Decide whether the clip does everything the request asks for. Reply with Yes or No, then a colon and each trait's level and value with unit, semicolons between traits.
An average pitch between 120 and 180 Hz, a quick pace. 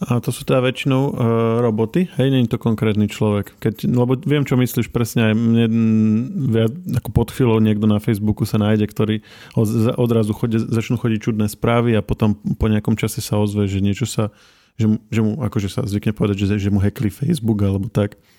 No: low, 110 Hz; fast, 200 wpm